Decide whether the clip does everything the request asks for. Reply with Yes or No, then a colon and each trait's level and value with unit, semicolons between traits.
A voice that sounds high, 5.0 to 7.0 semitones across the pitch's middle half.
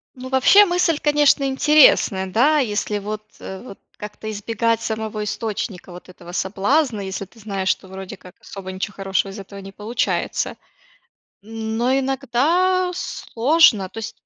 Yes: high, 220 Hz; wide, 5.4 semitones